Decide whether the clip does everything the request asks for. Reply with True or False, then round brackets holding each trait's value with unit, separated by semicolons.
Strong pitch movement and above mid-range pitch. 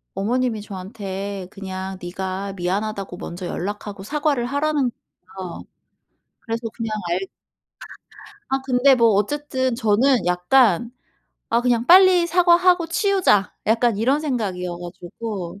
True (5.7 semitones; 225 Hz)